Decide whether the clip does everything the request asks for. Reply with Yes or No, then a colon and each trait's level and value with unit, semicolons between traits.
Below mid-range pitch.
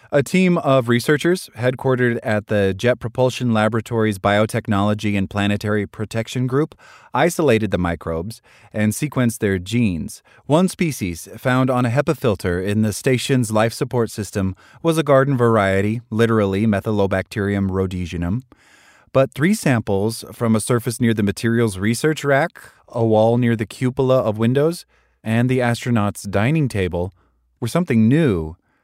Yes: low, 115 Hz